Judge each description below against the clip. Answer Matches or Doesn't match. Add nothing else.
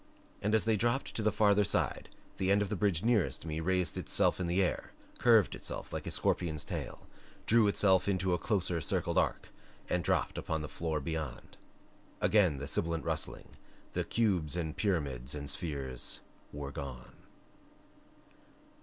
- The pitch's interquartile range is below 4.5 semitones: Doesn't match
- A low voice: Matches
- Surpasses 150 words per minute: Matches